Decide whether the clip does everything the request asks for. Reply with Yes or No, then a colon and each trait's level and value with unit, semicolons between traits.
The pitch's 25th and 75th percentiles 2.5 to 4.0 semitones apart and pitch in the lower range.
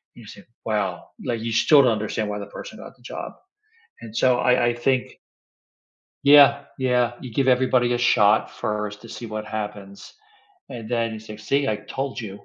Yes: average, 2.9 semitones; low, 115 Hz